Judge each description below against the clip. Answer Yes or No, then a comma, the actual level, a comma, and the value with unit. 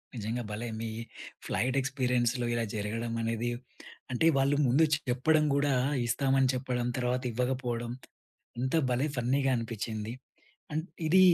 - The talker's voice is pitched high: No, low, 125 Hz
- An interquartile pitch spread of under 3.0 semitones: Yes, narrow, 2.4 semitones